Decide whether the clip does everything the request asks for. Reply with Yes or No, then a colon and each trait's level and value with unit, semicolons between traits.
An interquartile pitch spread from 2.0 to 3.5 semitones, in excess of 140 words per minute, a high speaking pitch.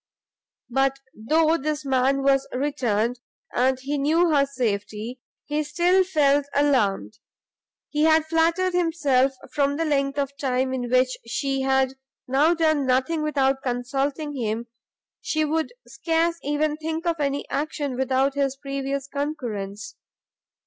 No: average, 2.8 semitones; slow, 135 wpm; very high, 275 Hz